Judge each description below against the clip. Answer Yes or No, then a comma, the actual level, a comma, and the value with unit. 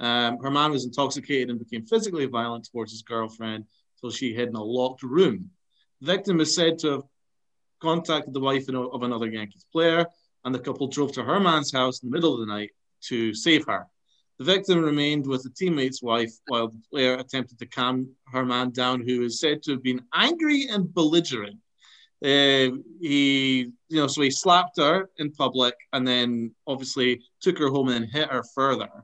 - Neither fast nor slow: Yes, average, 195 wpm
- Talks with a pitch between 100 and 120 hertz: No, low, 135 Hz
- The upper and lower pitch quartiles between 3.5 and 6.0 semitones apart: Yes, average, 3.9 semitones